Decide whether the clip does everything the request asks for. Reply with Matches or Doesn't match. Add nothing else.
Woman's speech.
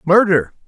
Doesn't match